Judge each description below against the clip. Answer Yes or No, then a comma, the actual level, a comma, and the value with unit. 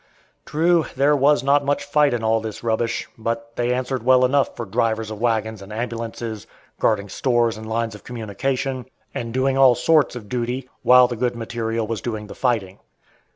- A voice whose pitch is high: No, low, 120 Hz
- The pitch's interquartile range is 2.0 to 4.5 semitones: Yes, narrow, 2.6 semitones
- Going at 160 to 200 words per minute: Yes, average, 185 wpm